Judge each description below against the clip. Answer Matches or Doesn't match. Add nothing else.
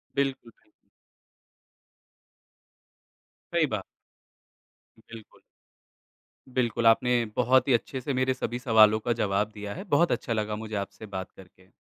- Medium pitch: Doesn't match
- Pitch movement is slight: Doesn't match